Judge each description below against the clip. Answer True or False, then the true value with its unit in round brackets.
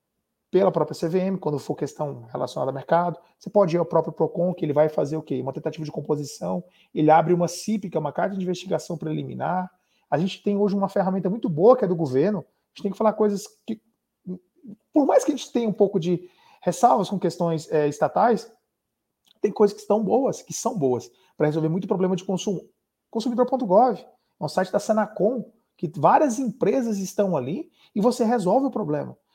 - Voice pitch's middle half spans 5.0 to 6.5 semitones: True (5.3 semitones)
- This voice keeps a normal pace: False (205 wpm)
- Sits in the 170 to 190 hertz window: True (185 Hz)